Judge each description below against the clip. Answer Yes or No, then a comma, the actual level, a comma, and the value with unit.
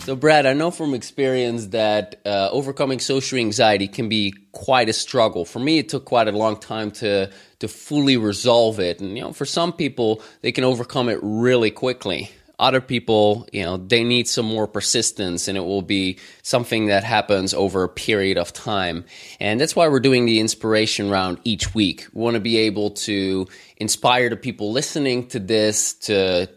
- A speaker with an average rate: Yes, average, 190 wpm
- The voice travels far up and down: No, average, 4.0 semitones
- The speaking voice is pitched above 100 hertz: Yes, low, 110 Hz